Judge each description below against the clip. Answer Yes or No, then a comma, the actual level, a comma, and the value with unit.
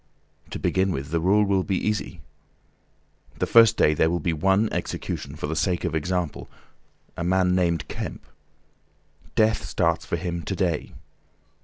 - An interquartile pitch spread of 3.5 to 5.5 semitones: No, average, 3.0 semitones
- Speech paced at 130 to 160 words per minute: Yes, average, 155 wpm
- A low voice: Yes, very low, 90 Hz